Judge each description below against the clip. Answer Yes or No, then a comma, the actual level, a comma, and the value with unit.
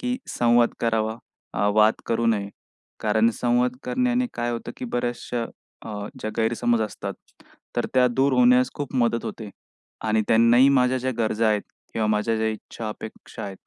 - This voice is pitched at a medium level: No, low, 115 Hz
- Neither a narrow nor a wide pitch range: No, narrow, 2.2 semitones